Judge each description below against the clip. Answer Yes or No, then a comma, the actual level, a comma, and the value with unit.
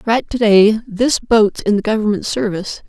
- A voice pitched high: Yes, high, 215 Hz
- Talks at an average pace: Yes, average, 190 wpm